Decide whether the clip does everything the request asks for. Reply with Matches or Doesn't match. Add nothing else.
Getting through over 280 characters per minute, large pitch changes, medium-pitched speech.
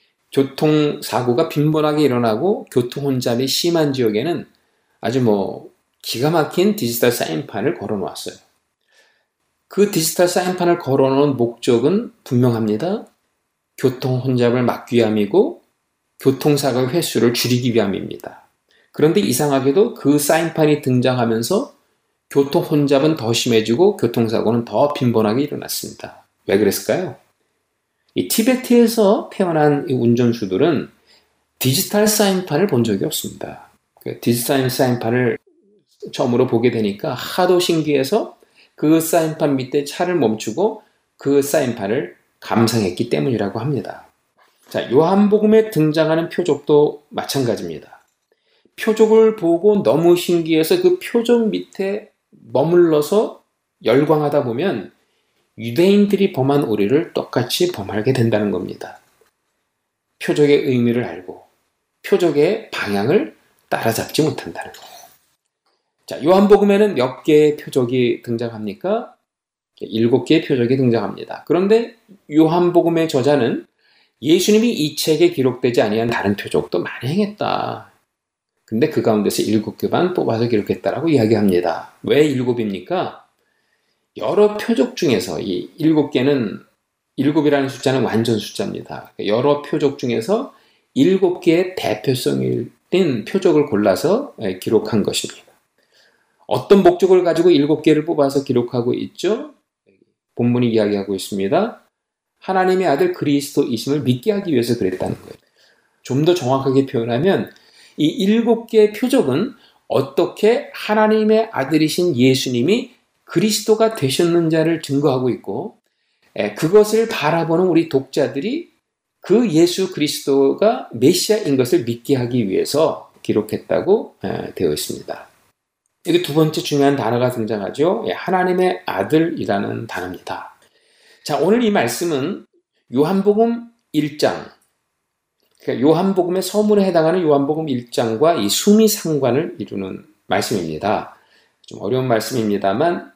Matches